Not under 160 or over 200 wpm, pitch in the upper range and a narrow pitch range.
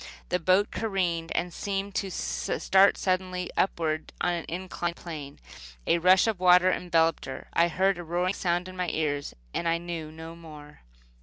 No: average, 170 wpm; medium, 175 Hz; narrow, 2.2 semitones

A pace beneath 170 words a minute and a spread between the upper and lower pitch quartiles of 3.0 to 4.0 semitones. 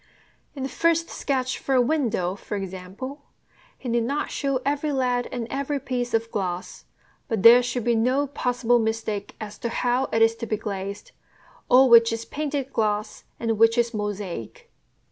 No: average, 175 wpm; average, 3.6 semitones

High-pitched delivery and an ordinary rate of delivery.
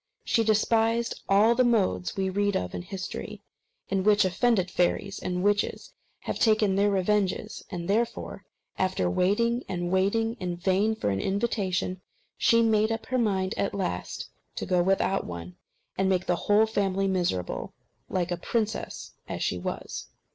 Yes: high, 195 Hz; average, 160 wpm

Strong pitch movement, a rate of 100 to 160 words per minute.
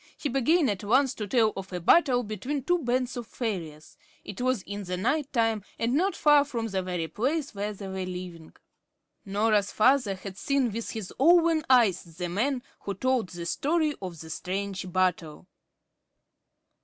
No: wide, 5.9 semitones; average, 175 wpm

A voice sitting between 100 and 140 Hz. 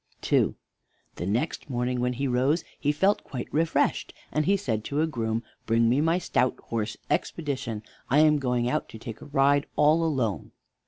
Yes: low, 135 Hz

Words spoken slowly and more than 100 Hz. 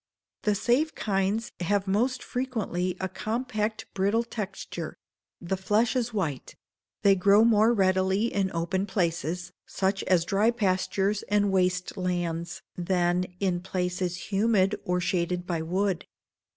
Yes: slow, 130 wpm; high, 190 Hz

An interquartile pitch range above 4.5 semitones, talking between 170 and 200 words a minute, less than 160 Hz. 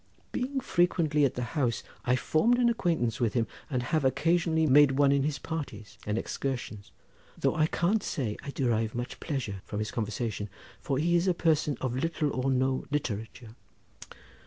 Yes: average, 5.2 semitones; average, 175 wpm; low, 135 Hz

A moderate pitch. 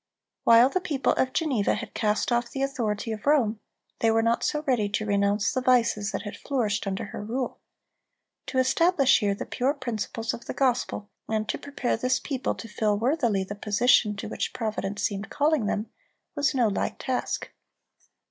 No: high, 230 Hz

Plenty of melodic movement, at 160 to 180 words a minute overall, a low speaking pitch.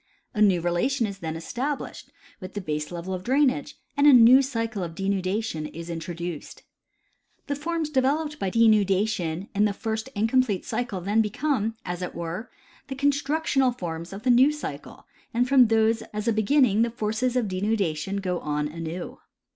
No: wide, 6.1 semitones; average, 165 wpm; high, 215 Hz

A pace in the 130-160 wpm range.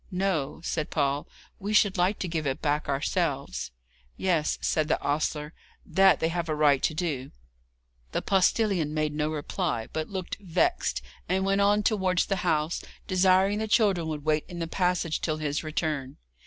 No: average, 170 wpm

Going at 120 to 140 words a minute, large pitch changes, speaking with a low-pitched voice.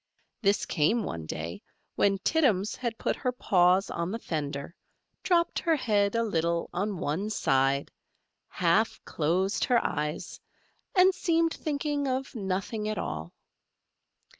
No: slow, 135 wpm; wide, 7.1 semitones; high, 200 Hz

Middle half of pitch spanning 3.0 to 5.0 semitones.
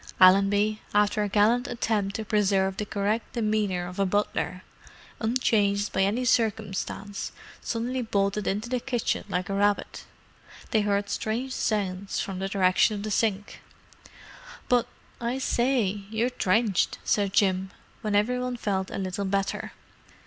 No: narrow, 2.4 semitones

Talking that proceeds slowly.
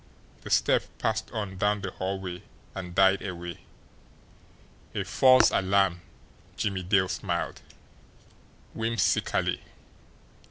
Yes: slow, 95 wpm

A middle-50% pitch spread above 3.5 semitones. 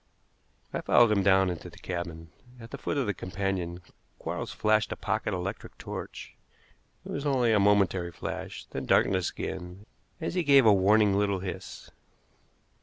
No: average, 2.9 semitones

